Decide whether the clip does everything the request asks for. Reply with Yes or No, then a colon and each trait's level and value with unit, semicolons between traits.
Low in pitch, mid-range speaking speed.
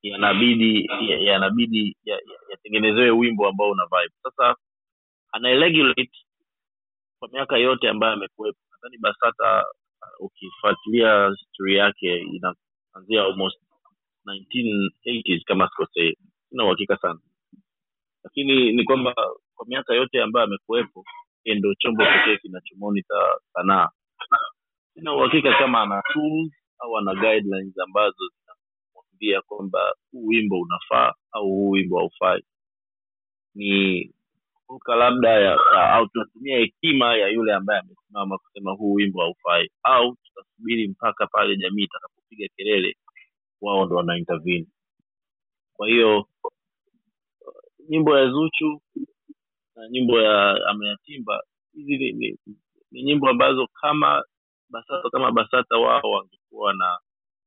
Yes: low, 115 Hz; average, 115 wpm